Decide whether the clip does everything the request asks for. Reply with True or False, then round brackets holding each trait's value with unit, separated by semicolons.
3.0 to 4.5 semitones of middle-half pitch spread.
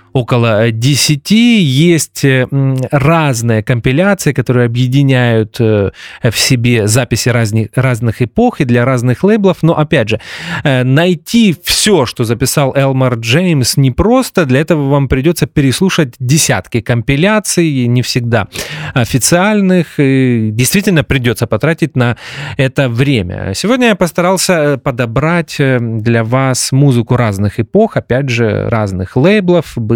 False (5.3 semitones)